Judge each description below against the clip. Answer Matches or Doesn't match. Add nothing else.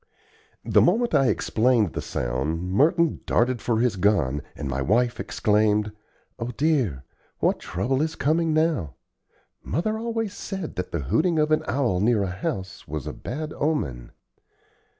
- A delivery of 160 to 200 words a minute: Doesn't match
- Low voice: Matches